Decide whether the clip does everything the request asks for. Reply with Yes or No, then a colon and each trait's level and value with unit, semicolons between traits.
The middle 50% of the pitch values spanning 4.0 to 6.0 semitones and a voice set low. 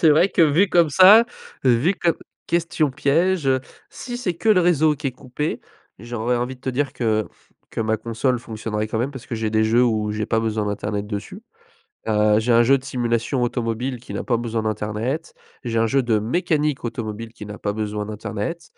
Yes: average, 5.1 semitones; low, 120 Hz